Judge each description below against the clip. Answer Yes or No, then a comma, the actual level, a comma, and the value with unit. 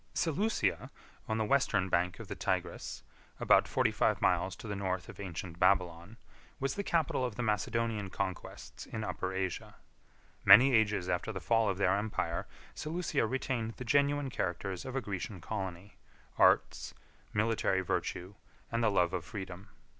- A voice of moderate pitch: No, low, 105 Hz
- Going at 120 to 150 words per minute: No, average, 165 wpm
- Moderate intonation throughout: Yes, average, 3.9 semitones